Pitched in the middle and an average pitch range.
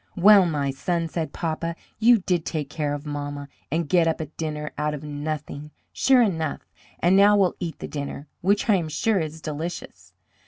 Yes: medium, 160 Hz; average, 3.3 semitones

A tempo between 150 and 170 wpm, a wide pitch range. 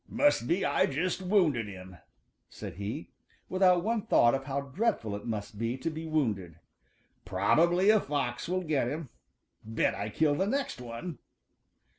Yes: average, 160 wpm; wide, 8.1 semitones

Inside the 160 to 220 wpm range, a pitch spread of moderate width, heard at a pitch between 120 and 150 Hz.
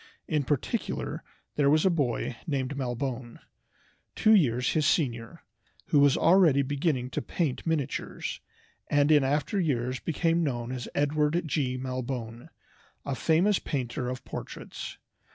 No: slow, 135 wpm; average, 3.7 semitones; medium, 140 Hz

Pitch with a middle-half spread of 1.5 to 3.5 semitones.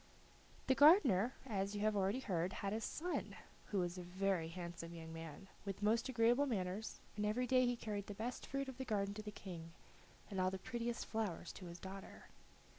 No: average, 4.3 semitones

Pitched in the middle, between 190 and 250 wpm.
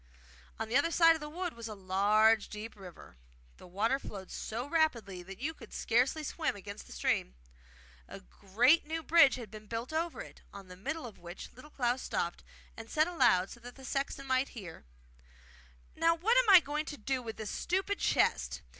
No: high, 245 Hz; average, 195 wpm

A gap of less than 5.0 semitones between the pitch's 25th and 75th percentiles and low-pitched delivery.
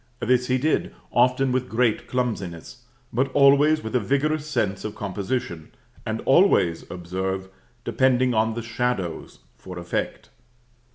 No: average, 5.3 semitones; low, 120 Hz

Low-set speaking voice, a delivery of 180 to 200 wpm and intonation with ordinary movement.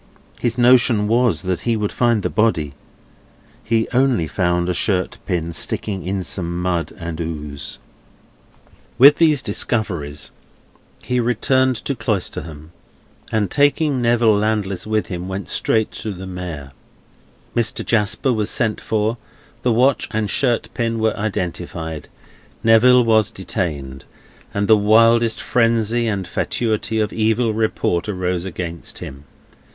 No: low, 105 Hz; slow, 135 wpm; average, 4.6 semitones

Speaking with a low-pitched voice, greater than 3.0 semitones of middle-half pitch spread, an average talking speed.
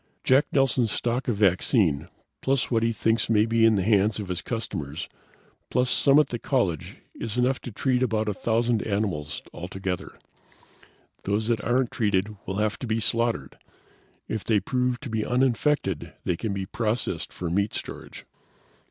Yes: low, 110 Hz; average, 3.8 semitones; average, 170 wpm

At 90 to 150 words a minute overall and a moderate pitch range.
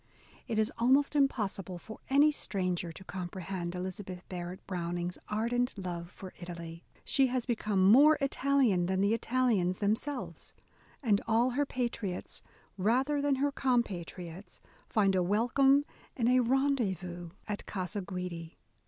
No: average, 140 wpm; wide, 5.8 semitones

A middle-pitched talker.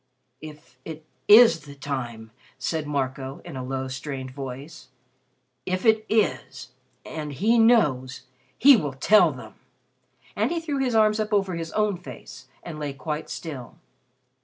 Yes: medium, 155 Hz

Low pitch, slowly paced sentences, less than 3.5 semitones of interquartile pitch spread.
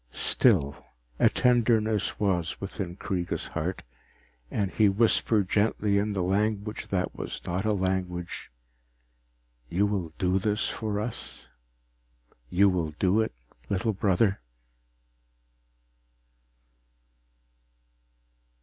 Yes: low, 100 Hz; slow, 100 wpm; narrow, 2.6 semitones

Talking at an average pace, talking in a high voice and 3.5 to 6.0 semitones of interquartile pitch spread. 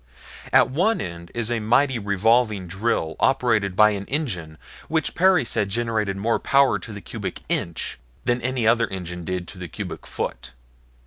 No: average, 170 wpm; low, 110 Hz; average, 4.7 semitones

